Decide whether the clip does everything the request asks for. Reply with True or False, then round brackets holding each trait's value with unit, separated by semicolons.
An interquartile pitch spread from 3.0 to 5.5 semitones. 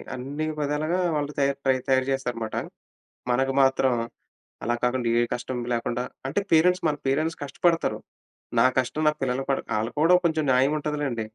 True (3.4 semitones)